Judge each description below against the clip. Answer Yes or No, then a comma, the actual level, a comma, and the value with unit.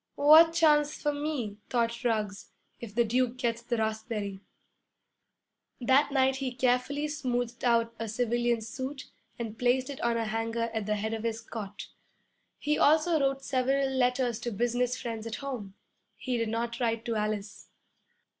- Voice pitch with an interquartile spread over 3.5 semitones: No, average, 2.8 semitones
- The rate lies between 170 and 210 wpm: No, average, 160 wpm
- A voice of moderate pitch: No, high, 240 Hz